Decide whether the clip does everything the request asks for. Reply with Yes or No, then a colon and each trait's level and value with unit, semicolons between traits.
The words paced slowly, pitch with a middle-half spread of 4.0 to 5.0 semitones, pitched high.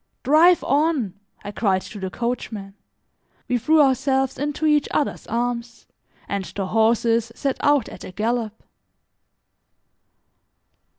Yes: slow, 120 wpm; average, 4.6 semitones; high, 240 Hz